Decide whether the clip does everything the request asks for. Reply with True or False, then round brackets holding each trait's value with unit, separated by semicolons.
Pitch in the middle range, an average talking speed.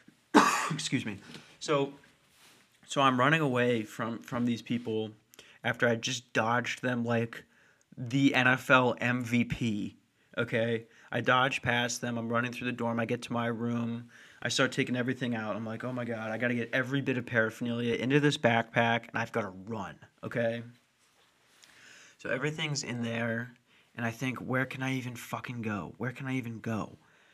False (120 Hz; 170 wpm)